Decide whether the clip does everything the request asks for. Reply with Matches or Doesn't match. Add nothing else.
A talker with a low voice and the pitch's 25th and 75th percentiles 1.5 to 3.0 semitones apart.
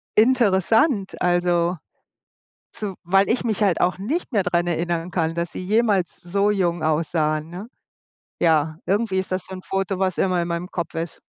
Doesn't match